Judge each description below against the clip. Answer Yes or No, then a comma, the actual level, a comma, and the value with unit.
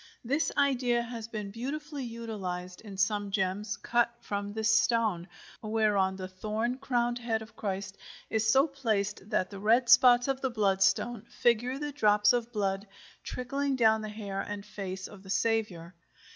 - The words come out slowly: No, average, 160 wpm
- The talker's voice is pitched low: No, high, 220 Hz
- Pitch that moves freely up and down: No, average, 3.3 semitones